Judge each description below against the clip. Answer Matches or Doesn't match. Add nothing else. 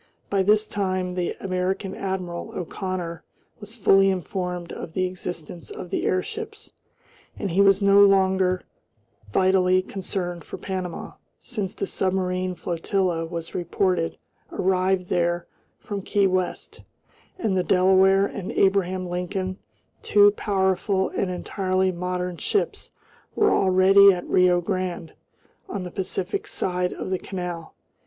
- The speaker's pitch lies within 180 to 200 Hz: Matches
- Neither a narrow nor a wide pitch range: Doesn't match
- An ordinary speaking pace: Doesn't match